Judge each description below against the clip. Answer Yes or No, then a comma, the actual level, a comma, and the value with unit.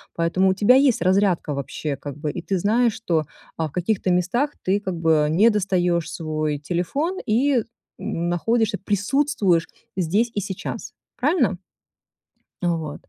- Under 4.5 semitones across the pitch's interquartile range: No, average, 5.1 semitones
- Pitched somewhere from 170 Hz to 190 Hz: Yes, medium, 185 Hz